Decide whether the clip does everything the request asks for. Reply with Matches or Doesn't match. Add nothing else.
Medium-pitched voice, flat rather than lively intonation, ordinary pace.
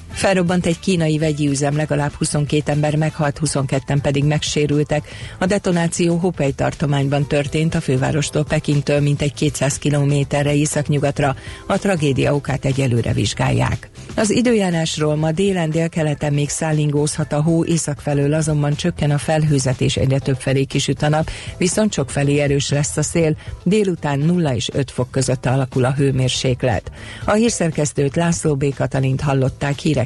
Matches